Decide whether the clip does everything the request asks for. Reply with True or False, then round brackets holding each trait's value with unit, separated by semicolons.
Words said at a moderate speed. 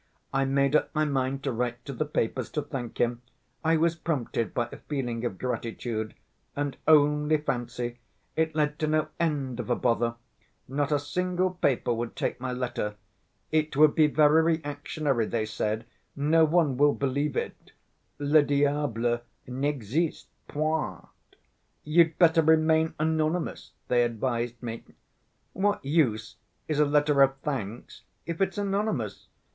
True (150 wpm)